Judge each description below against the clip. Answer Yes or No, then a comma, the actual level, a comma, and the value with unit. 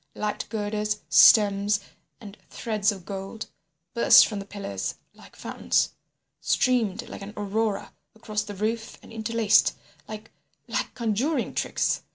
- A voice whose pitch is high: Yes, high, 210 Hz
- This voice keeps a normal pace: No, slow, 125 wpm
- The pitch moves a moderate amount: No, narrow, 1.7 semitones